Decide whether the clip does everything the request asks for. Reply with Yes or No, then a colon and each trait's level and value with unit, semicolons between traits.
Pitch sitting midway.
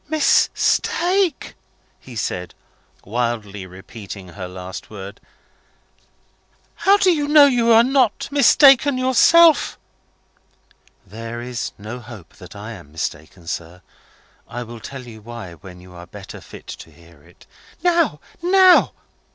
No: low, 120 Hz